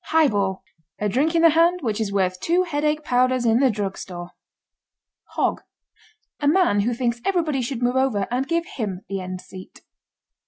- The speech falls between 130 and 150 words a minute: No, average, 170 wpm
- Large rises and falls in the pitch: Yes, wide, 7.1 semitones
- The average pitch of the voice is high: Yes, high, 245 Hz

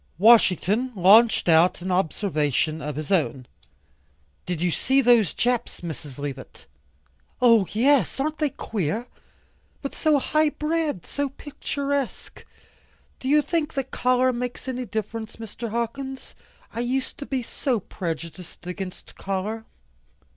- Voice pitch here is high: Yes, high, 230 Hz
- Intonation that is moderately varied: No, wide, 6.7 semitones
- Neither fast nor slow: No, slow, 130 wpm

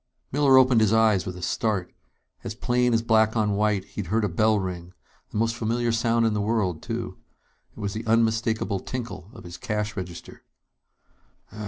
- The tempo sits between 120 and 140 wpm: No, average, 180 wpm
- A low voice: Yes, low, 110 Hz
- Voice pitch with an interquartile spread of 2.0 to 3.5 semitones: Yes, narrow, 2.5 semitones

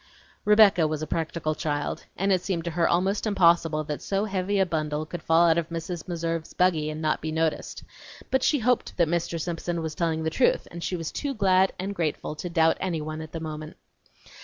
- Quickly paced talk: Yes, fast, 210 wpm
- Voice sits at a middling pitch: Yes, medium, 170 Hz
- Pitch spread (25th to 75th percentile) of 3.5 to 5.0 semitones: No, average, 2.8 semitones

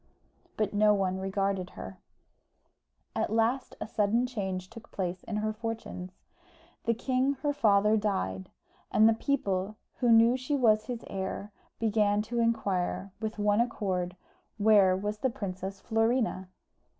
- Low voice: No, high, 210 Hz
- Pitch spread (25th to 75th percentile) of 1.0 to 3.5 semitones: Yes, average, 3.0 semitones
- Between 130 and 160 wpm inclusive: Yes, average, 140 wpm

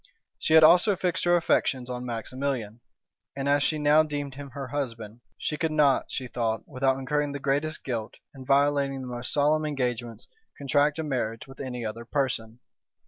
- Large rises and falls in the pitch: No, average, 3.1 semitones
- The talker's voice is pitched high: No, low, 135 Hz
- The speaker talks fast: No, average, 180 wpm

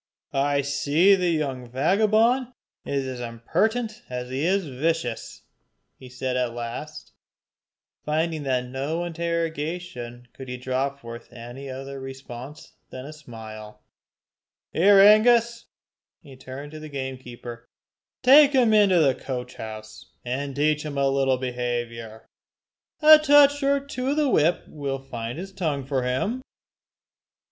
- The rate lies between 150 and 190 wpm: No, average, 140 wpm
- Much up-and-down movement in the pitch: Yes, wide, 6.0 semitones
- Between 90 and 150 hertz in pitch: Yes, medium, 140 Hz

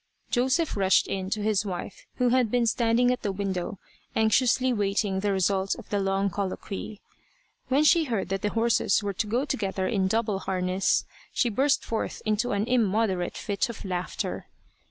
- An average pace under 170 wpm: No, average, 175 wpm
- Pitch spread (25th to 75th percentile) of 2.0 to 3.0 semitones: No, average, 3.6 semitones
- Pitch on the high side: Yes, high, 210 Hz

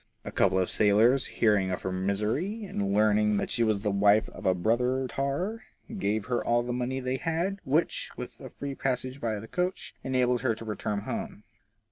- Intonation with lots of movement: No, average, 4.2 semitones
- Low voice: Yes, low, 120 Hz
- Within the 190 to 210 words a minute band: Yes, average, 195 wpm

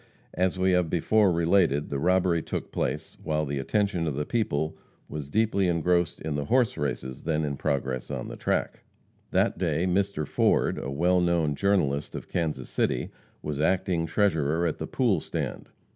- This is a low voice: Yes, very low, 85 Hz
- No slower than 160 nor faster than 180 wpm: Yes, average, 175 wpm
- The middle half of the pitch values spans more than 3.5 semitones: Yes, average, 4.0 semitones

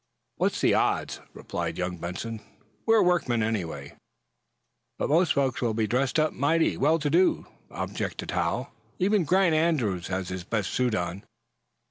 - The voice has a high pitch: No, low, 125 Hz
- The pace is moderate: Yes, average, 150 wpm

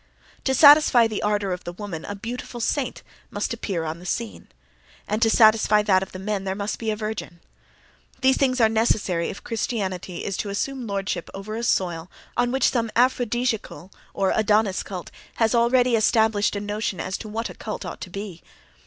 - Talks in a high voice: Yes, high, 210 Hz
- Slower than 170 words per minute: No, average, 190 wpm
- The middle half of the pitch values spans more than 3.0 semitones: Yes, average, 3.4 semitones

